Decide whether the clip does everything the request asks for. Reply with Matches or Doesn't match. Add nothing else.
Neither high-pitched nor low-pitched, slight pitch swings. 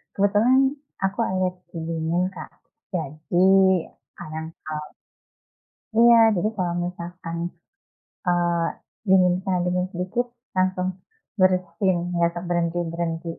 Matches